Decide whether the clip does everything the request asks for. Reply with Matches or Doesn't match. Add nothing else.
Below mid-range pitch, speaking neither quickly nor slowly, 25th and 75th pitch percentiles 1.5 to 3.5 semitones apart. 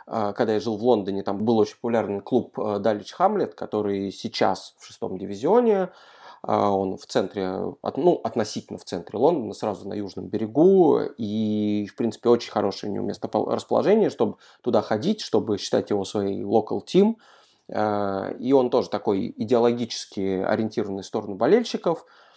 Matches